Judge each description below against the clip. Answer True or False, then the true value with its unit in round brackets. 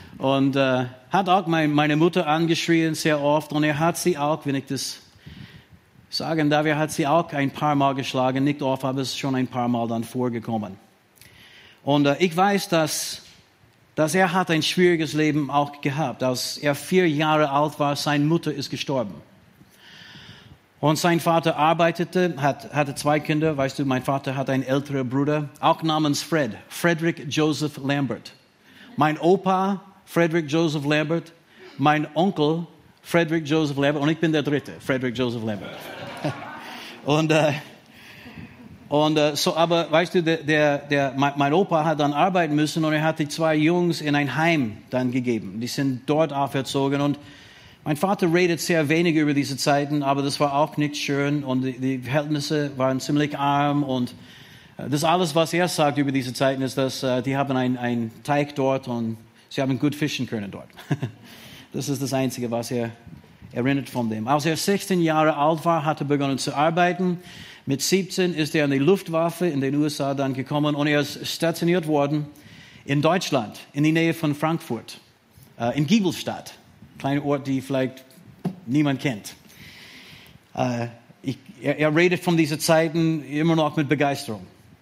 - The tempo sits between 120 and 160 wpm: False (170 wpm)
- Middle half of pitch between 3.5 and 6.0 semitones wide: False (3.1 semitones)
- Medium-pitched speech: True (145 Hz)